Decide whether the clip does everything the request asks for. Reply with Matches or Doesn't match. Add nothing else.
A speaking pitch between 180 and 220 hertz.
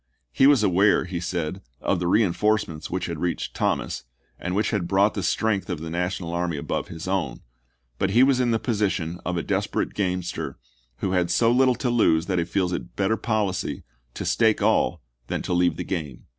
Doesn't match